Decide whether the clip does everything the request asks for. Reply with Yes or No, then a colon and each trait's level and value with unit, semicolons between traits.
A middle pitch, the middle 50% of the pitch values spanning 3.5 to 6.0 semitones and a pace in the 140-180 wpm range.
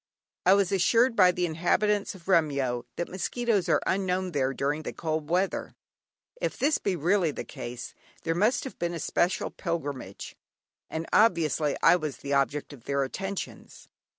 Yes: medium, 170 Hz; average, 4.8 semitones; average, 165 wpm